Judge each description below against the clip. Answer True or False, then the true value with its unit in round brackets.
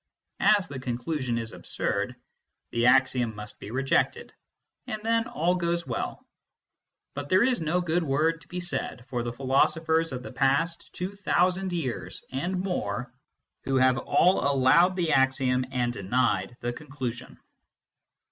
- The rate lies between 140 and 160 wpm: True (150 wpm)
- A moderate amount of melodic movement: False (5.7 semitones)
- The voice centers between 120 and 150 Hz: True (140 Hz)